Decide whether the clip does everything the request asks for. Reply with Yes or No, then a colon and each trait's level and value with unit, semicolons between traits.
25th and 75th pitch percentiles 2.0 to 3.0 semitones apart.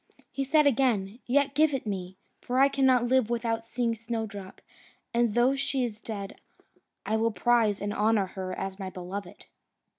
No: average, 4.0 semitones